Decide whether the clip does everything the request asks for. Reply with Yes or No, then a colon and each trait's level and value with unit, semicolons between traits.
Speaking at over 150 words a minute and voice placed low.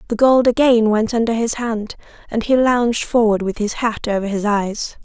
No: average, 200 wpm; high, 225 Hz